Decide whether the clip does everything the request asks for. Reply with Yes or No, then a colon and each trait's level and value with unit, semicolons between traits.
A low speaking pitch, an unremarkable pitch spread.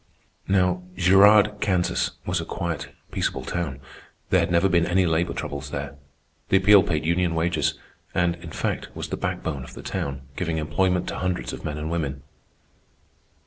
Yes: very low, 85 Hz; average, 3.1 semitones